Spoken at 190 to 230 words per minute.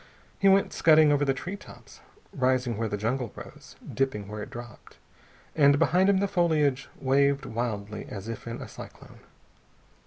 No: average, 165 wpm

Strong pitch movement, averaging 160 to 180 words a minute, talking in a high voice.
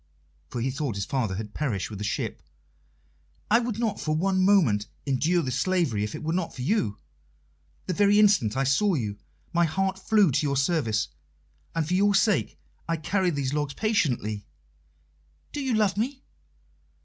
No: wide, 7.7 semitones; average, 175 wpm; medium, 155 Hz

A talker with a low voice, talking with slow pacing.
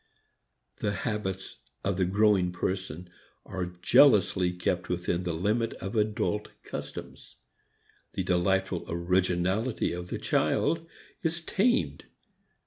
Yes: very low, 95 Hz; slow, 110 wpm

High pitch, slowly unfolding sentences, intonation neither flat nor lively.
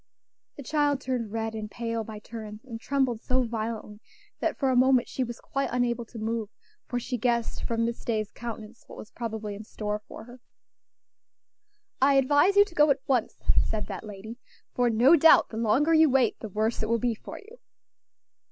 No: high, 235 Hz; average, 195 wpm; average, 3.1 semitones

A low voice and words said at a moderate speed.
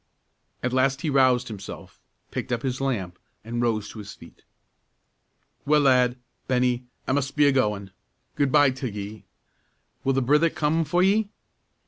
Yes: low, 130 Hz; average, 160 wpm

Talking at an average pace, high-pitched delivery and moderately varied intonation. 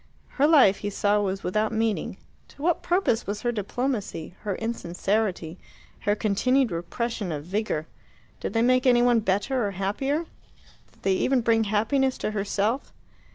Yes: average, 155 wpm; high, 215 Hz; average, 3.9 semitones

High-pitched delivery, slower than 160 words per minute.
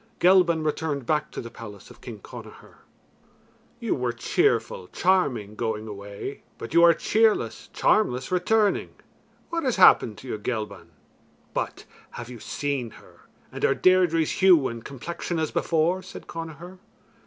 No: medium, 155 Hz; average, 145 wpm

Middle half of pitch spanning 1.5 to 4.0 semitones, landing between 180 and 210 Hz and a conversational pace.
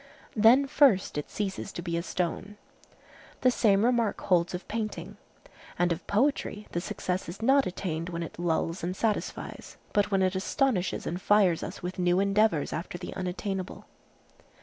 Yes: average, 3.3 semitones; high, 190 Hz; average, 165 wpm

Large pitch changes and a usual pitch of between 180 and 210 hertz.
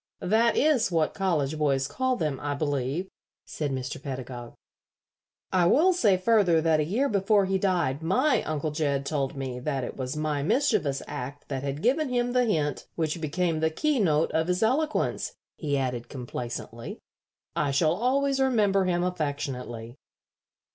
No: wide, 6.7 semitones; medium, 160 Hz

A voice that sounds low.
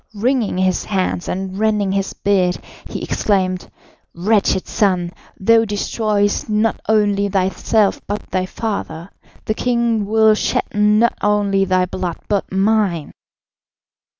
No: high, 200 Hz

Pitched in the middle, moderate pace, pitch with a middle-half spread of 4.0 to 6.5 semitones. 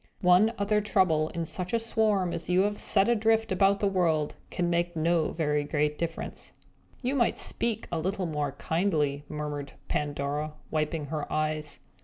Yes: medium, 170 Hz; average, 165 wpm; average, 4.7 semitones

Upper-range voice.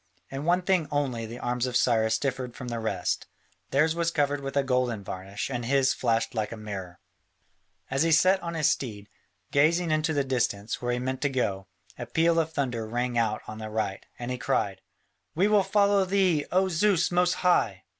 No: low, 130 Hz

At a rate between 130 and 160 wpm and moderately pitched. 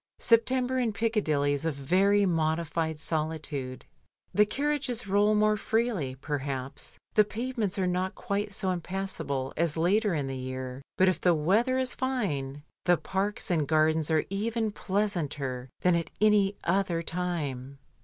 Yes: average, 150 wpm; medium, 180 Hz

